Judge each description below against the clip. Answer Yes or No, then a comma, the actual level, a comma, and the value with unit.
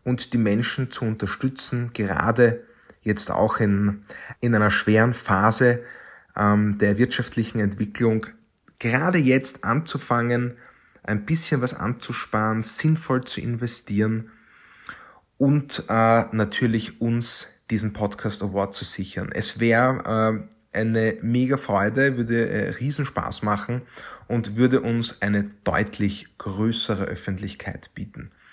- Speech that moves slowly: Yes, slow, 115 wpm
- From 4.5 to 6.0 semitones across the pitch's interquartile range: No, average, 2.8 semitones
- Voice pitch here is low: Yes, low, 115 Hz